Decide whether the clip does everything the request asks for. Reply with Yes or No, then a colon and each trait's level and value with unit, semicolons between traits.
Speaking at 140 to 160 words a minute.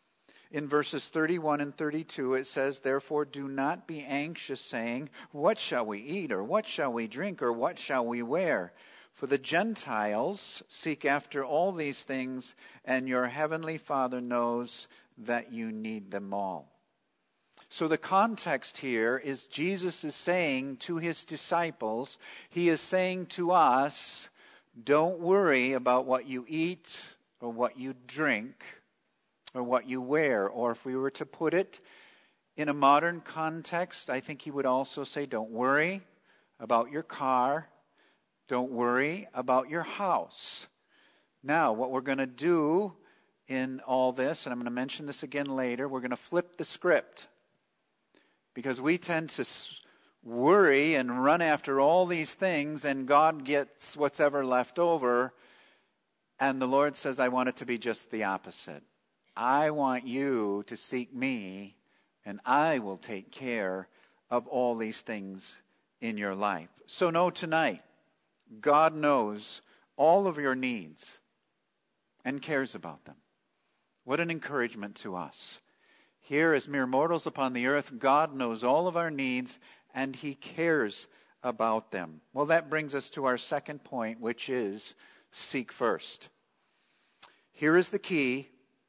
Yes: average, 150 wpm